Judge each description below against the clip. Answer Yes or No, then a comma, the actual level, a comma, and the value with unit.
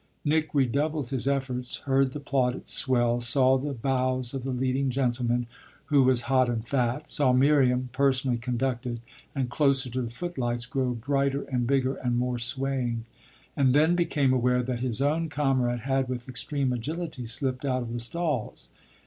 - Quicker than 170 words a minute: No, average, 165 wpm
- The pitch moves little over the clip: Yes, narrow, 2.1 semitones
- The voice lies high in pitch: No, low, 130 Hz